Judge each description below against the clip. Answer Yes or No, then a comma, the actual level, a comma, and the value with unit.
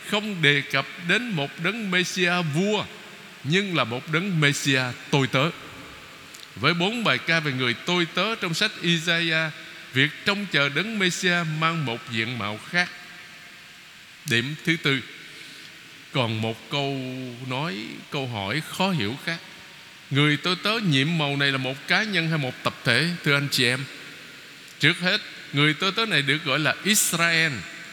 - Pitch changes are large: No, average, 4.2 semitones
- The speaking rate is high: No, slow, 165 wpm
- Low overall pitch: No, medium, 160 Hz